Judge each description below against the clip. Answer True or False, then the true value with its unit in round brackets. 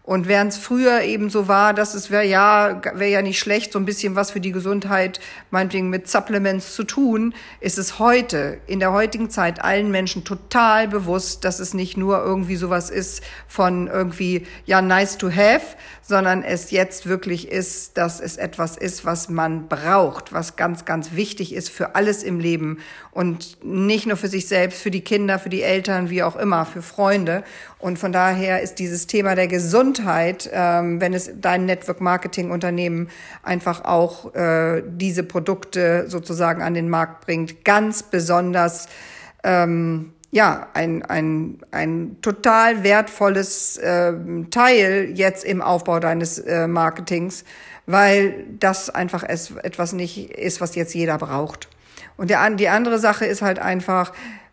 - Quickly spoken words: False (160 wpm)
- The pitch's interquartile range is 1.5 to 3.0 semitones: True (2.6 semitones)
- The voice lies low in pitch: False (185 Hz)